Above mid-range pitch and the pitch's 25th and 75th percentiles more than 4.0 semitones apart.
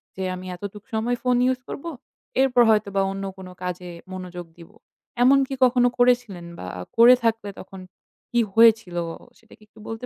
Yes: high, 220 Hz; average, 4.6 semitones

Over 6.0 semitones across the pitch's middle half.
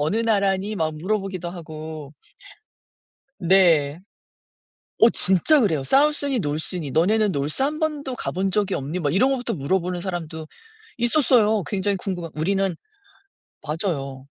No: wide, 5.4 semitones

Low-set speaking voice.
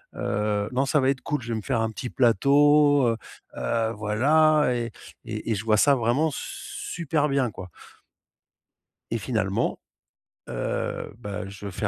Yes: low, 120 Hz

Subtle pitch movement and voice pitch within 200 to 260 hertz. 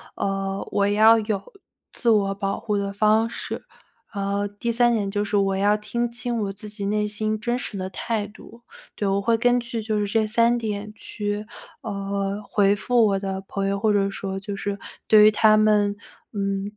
Yes: narrow, 1.7 semitones; high, 205 Hz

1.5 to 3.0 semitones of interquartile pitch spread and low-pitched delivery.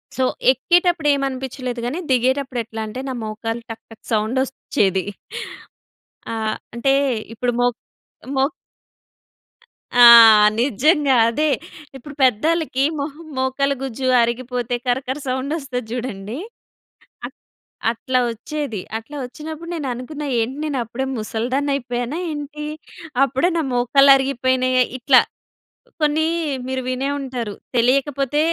No: average, 2.7 semitones; very high, 260 Hz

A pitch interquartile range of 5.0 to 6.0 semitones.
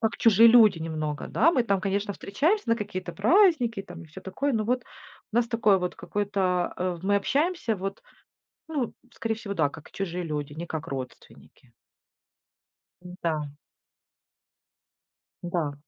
Yes: average, 5.3 semitones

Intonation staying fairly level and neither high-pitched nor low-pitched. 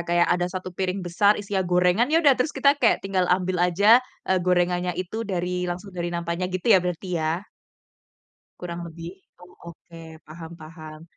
Yes: narrow, 1.7 semitones; medium, 180 Hz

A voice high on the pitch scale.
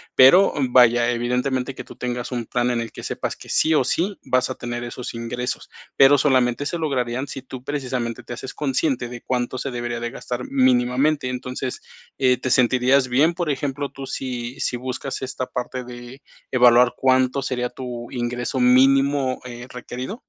No: low, 125 Hz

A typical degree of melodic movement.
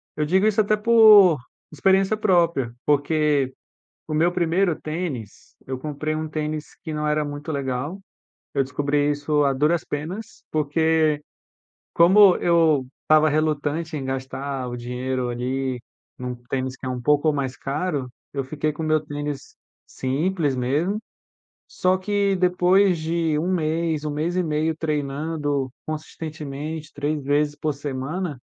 Yes: average, 3.1 semitones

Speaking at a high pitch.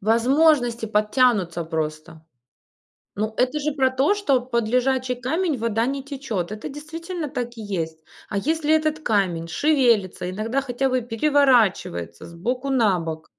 Yes: high, 245 Hz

